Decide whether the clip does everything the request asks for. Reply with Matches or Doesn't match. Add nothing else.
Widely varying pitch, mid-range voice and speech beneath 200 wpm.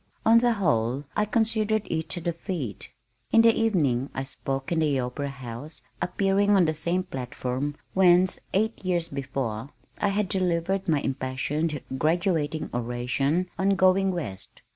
Matches